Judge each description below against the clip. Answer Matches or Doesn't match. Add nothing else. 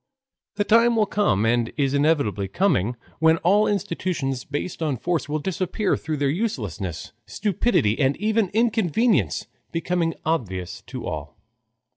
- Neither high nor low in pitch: Matches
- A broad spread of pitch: Matches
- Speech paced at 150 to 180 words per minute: Doesn't match